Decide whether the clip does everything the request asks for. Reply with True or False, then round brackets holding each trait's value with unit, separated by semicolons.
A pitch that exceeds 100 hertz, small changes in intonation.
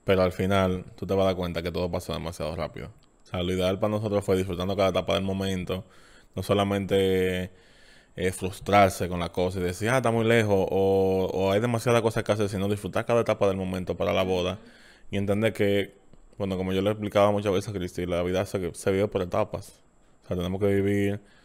False (95 Hz; 1.7 semitones)